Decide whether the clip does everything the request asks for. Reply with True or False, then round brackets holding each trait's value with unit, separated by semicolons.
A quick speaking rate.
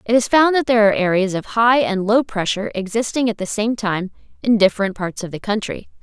True (230 wpm)